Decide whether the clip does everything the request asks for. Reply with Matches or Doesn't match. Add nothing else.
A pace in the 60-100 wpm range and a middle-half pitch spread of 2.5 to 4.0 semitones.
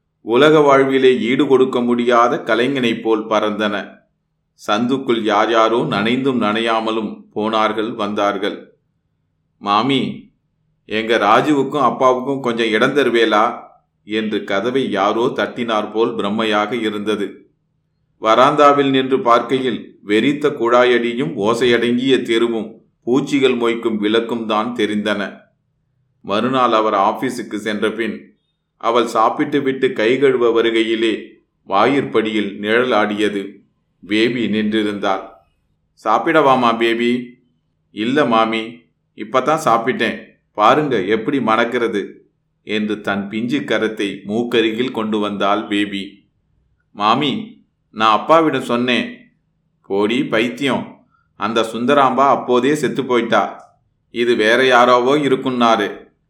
Matches